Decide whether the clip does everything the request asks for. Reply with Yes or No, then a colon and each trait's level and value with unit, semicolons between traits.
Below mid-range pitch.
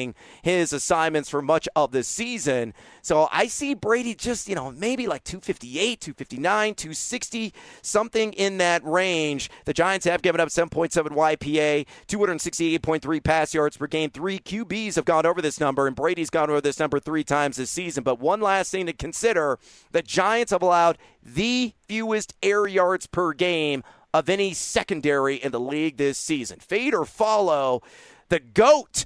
No: medium, 170 Hz